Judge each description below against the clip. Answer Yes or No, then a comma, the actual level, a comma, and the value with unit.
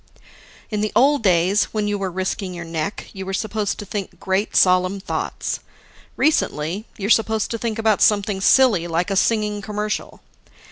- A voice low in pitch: No, high, 205 Hz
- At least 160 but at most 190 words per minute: Yes, average, 170 wpm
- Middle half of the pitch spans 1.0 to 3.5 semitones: Yes, narrow, 2.4 semitones